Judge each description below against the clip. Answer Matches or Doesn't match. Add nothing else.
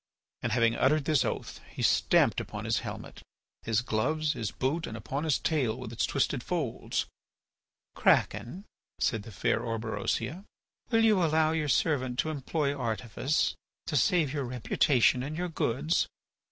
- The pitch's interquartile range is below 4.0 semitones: Doesn't match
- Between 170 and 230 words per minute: Doesn't match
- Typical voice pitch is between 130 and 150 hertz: Matches